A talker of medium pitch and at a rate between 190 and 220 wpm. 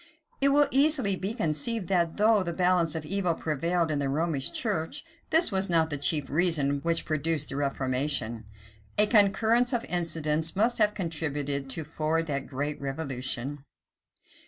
No: medium, 165 Hz; average, 160 wpm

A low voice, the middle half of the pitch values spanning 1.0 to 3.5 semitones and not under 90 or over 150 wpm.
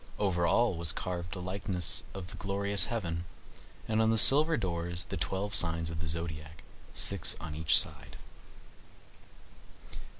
Yes: very low, 90 Hz; average, 3.2 semitones; average, 145 wpm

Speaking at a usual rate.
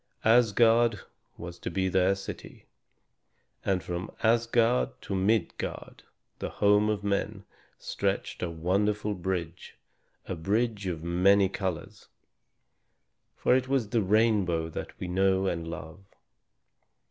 No: slow, 120 wpm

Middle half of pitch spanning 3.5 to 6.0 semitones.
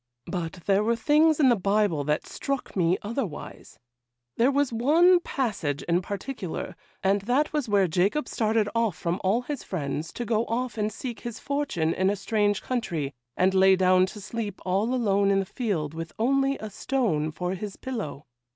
Yes: average, 4.9 semitones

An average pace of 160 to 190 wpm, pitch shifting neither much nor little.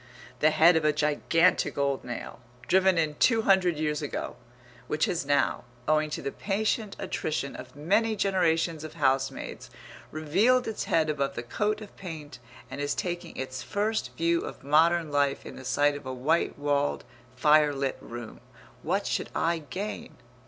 Yes: average, 165 wpm; average, 4.0 semitones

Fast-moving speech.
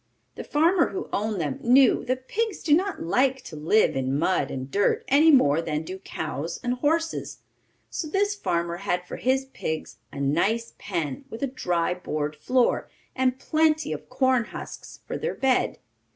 No: average, 175 wpm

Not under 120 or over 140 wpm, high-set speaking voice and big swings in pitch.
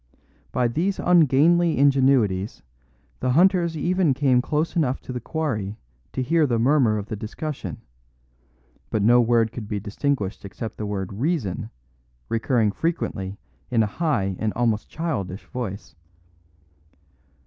No: slow, 135 wpm; low, 125 Hz; wide, 6.2 semitones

